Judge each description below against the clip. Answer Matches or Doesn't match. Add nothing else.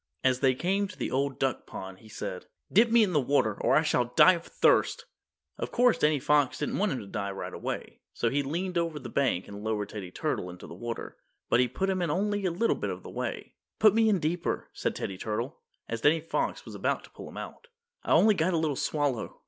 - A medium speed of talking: Doesn't match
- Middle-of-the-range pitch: Matches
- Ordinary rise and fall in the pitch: Doesn't match